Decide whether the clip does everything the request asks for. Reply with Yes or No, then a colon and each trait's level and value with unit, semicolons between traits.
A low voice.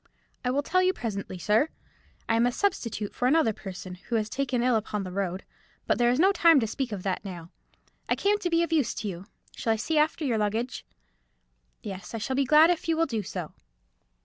No: high, 235 Hz